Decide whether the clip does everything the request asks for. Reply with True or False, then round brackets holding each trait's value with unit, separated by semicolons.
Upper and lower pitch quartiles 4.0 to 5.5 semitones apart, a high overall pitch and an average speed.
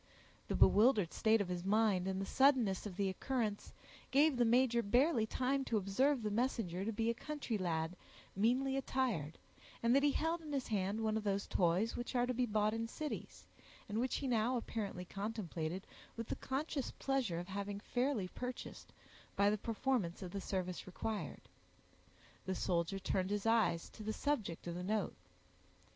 True (4.7 semitones; 220 Hz; 180 wpm)